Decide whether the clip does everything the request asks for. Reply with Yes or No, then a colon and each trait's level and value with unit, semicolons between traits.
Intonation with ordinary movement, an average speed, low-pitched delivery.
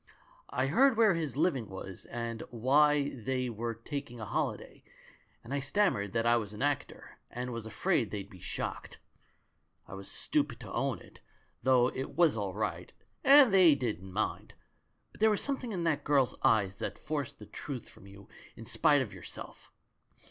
No: wide, 5.7 semitones; average, 180 wpm; low, 125 Hz